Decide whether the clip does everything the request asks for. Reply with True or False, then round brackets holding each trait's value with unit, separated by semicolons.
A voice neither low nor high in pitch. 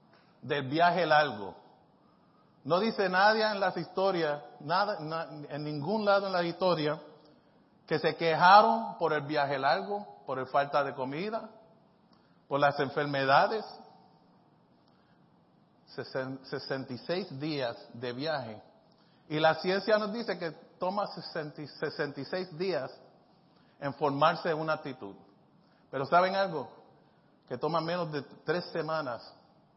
True (155 Hz)